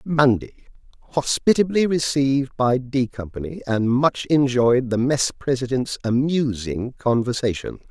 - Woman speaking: No, male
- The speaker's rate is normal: No, slow, 100 wpm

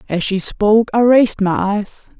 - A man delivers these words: No, female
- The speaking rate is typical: Yes, average, 190 wpm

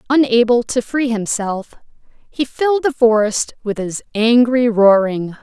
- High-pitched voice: Yes, high, 235 Hz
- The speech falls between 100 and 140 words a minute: Yes, slow, 135 wpm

